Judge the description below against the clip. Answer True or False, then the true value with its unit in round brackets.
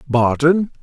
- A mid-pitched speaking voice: True (145 Hz)